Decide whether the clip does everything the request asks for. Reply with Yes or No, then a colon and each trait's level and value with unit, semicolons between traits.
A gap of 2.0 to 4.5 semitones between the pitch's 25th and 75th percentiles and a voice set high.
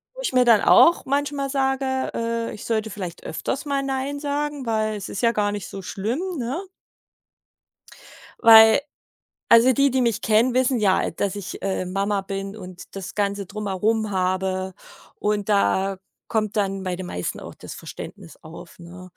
No: average, 4.9 semitones; high, 215 Hz